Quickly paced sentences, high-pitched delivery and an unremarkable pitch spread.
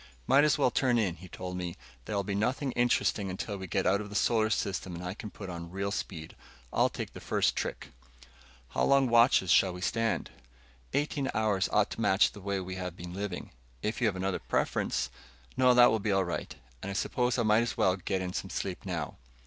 No: fast, 225 wpm; low, 100 Hz; average, 3.7 semitones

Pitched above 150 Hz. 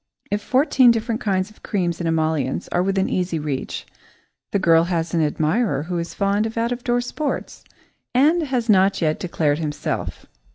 Yes: medium, 185 Hz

